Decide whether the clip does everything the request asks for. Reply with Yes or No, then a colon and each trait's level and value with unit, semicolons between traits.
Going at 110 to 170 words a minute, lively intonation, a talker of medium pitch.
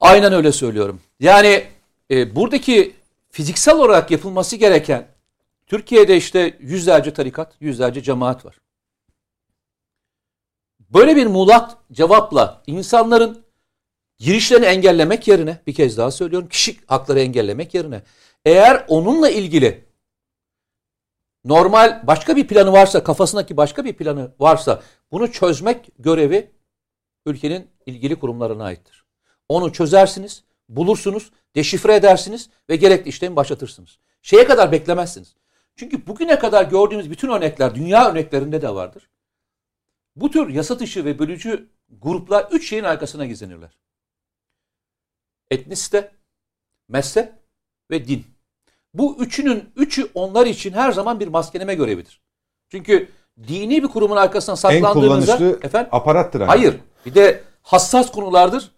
Yes: average, 115 wpm; wide, 7.9 semitones; medium, 180 Hz